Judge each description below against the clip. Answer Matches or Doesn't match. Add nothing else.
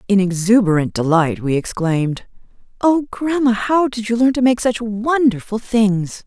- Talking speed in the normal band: Matches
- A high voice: Matches